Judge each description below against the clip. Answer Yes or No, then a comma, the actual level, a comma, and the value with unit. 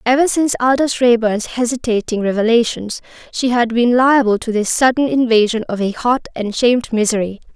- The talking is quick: No, average, 160 wpm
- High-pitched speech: Yes, high, 235 Hz